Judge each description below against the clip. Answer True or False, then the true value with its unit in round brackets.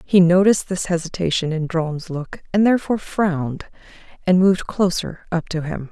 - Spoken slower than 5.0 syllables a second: False (5.3 syllables/s)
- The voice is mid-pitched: True (175 Hz)